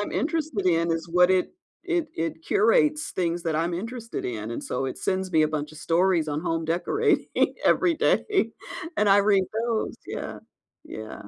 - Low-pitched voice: No, medium, 185 Hz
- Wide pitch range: Yes, wide, 6.6 semitones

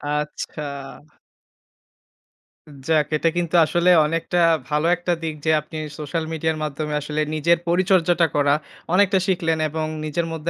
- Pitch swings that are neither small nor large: No, narrow, 2.2 semitones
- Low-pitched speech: No, medium, 160 Hz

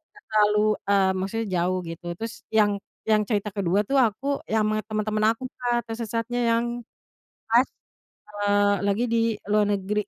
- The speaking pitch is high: Yes, high, 210 Hz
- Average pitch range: No, narrow, 2.0 semitones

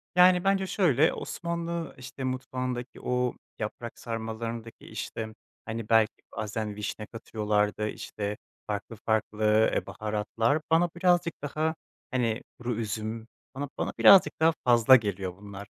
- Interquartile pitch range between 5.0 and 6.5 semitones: Yes, average, 5.3 semitones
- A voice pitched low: Yes, low, 115 Hz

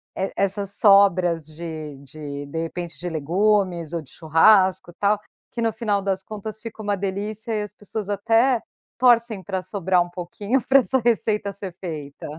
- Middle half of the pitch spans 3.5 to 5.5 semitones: Yes, average, 3.8 semitones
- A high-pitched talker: Yes, high, 195 Hz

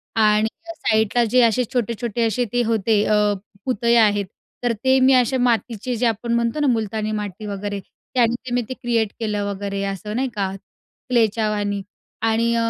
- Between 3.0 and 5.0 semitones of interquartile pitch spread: No, narrow, 2.4 semitones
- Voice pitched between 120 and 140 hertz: No, high, 225 Hz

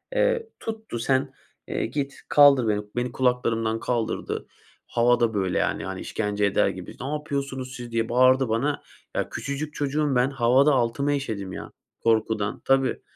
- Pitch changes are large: No, average, 3.6 semitones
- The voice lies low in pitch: Yes, low, 125 Hz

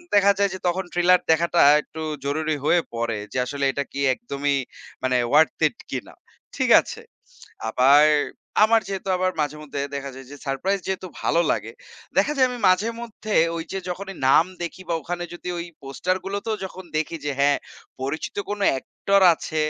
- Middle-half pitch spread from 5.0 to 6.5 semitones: Yes, average, 5.3 semitones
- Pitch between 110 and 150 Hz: No, medium, 170 Hz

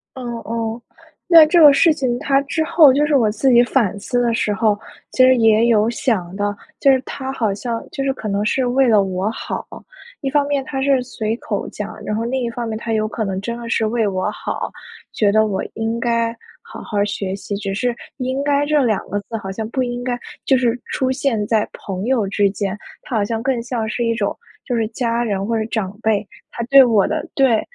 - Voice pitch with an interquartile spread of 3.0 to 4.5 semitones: Yes, average, 3.5 semitones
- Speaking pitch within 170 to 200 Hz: No, high, 230 Hz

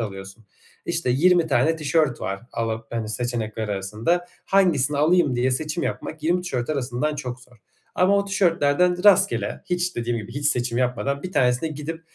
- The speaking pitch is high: No, medium, 140 Hz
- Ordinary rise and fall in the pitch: No, wide, 5.9 semitones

